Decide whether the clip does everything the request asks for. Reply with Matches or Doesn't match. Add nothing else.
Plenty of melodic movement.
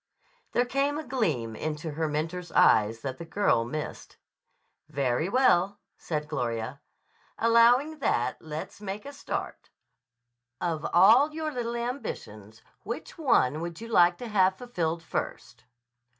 Matches